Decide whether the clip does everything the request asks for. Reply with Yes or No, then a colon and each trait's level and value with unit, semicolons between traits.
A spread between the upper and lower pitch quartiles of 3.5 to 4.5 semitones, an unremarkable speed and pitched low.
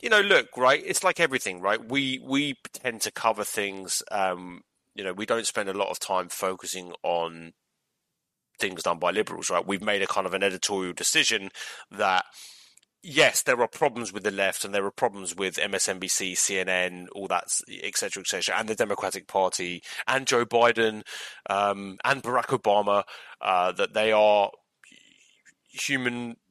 Yes: average, 4.1 semitones; average, 170 wpm; low, 100 Hz